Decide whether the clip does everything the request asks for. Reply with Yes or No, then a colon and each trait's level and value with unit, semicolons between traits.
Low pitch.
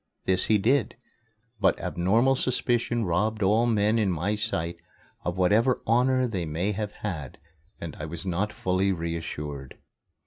Yes: low, 100 Hz